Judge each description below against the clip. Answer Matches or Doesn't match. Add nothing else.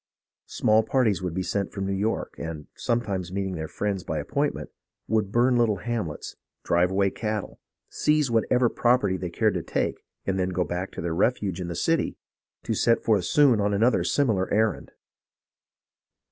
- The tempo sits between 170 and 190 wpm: Matches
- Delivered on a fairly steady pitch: Doesn't match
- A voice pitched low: Matches